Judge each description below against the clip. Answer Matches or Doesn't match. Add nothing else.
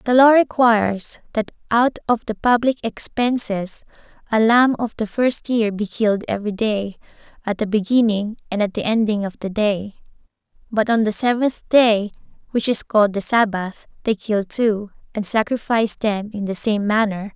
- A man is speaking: Doesn't match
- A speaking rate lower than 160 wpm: Doesn't match